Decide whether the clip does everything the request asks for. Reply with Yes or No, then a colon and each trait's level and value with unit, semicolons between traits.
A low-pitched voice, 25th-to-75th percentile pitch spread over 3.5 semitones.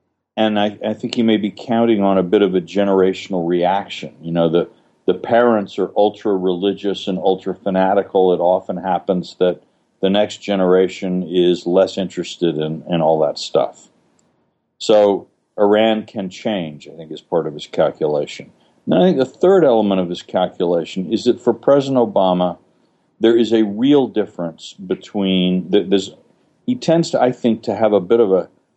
No: low, 100 Hz; average, 3.2 semitones